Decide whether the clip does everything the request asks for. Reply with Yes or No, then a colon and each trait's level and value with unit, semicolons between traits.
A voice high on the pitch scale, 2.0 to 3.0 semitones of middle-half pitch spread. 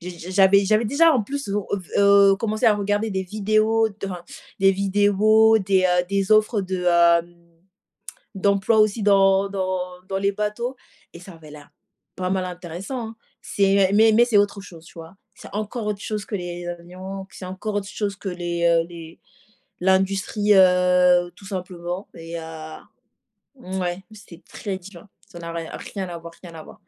Yes: high, 195 Hz; average, 2.7 semitones